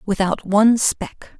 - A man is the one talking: No, female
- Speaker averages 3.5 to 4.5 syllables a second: Yes, 4.0 syllables/s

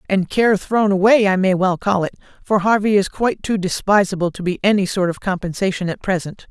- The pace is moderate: No, fast, 210 wpm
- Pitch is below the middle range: No, high, 195 Hz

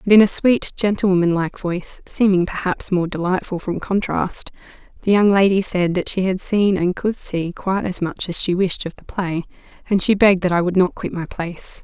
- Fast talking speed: Yes, fast, 215 wpm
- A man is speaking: No, female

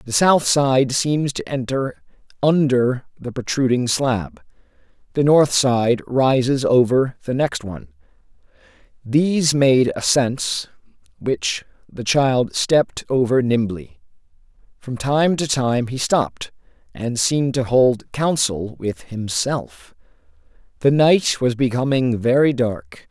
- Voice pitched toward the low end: Yes, low, 125 Hz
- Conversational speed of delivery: No, slow, 120 wpm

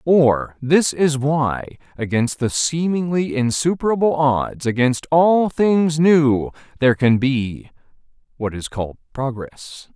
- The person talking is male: Yes, male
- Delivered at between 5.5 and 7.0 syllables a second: No, 3.7 syllables/s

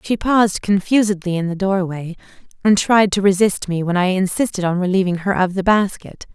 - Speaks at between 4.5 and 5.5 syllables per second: Yes, 5.4 syllables/s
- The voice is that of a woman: Yes, female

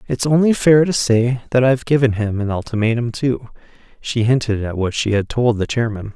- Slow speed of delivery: No, fast, 205 wpm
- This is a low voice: Yes, low, 120 Hz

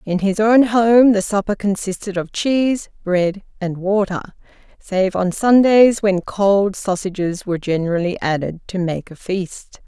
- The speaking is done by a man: No, female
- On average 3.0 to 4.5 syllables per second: Yes, 4.3 syllables/s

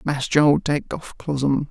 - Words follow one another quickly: No, average, 175 wpm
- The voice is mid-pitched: Yes, medium, 145 Hz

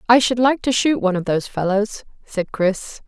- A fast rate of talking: Yes, fast, 215 wpm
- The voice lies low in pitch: No, high, 215 Hz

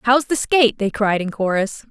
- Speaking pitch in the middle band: No, high, 225 Hz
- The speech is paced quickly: Yes, fast, 220 wpm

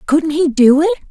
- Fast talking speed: Yes, fast, 215 wpm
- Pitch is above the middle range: Yes, very high, 290 Hz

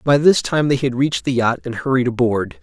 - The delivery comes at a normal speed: No, fast, 250 wpm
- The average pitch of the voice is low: Yes, low, 130 Hz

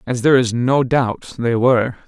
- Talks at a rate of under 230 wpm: Yes, fast, 205 wpm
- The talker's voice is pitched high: No, low, 125 Hz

